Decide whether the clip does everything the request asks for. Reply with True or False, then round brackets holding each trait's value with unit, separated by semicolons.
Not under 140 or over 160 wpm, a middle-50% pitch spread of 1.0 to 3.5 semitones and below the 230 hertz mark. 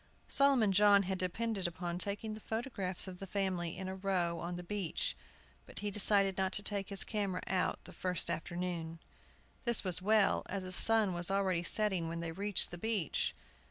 False (190 wpm; 2.6 semitones; 190 Hz)